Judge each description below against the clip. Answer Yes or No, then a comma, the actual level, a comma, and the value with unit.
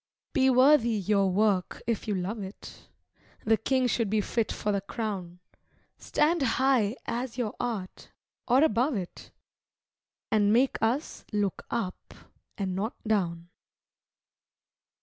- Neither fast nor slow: No, slow, 130 wpm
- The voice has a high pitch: Yes, high, 220 Hz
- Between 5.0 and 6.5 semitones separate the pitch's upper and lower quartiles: No, average, 3.8 semitones